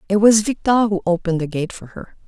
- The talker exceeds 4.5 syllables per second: Yes, 6.1 syllables/s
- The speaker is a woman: Yes, female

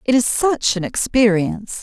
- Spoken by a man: No, female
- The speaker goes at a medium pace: Yes, average, 165 wpm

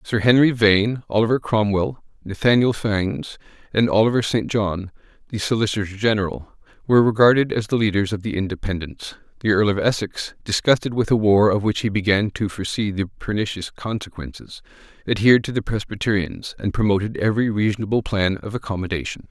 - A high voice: No, low, 105 Hz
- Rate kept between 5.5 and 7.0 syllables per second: Yes, 5.8 syllables/s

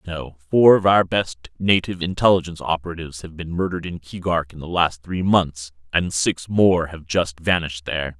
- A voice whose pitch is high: No, very low, 85 Hz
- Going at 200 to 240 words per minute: No, average, 190 wpm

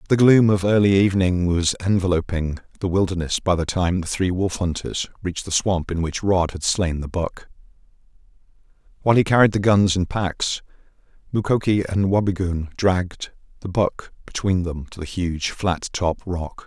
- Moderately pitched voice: No, very low, 90 Hz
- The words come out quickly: No, average, 170 wpm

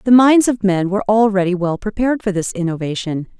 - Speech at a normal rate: Yes, average, 195 wpm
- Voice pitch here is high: Yes, high, 200 Hz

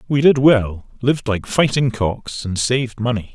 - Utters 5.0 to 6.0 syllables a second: No, 4.6 syllables/s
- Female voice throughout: No, male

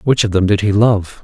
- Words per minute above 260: Yes, fast, 290 wpm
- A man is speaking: Yes, male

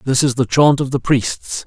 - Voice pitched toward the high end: No, low, 130 Hz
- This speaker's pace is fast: Yes, fast, 250 wpm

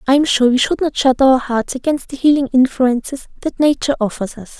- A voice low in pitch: No, very high, 260 Hz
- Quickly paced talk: Yes, fast, 220 wpm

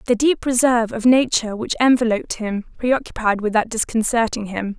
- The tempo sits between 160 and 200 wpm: No, average, 150 wpm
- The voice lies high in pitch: Yes, high, 230 Hz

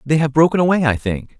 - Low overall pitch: No, medium, 145 Hz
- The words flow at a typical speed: No, fast, 255 wpm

